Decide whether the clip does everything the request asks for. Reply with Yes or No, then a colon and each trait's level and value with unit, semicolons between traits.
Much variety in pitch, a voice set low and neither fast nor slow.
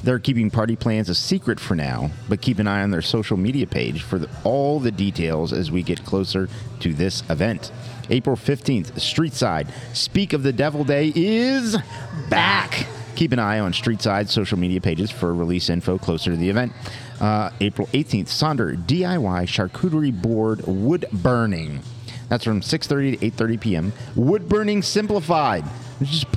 Yes: wide, 5.7 semitones; low, 115 Hz; average, 175 wpm